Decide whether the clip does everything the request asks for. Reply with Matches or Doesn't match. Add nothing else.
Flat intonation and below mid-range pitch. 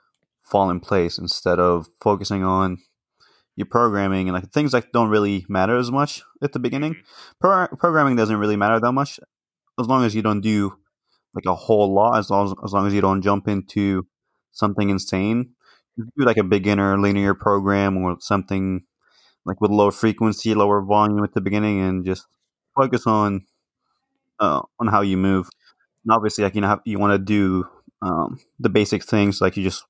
Matches